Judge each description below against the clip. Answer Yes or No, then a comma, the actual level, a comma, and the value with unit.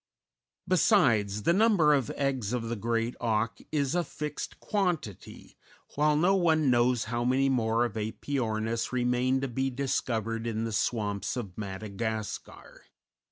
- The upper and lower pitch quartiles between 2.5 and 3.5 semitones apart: No, average, 4.0 semitones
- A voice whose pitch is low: Yes, low, 120 Hz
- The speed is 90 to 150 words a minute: Yes, average, 140 wpm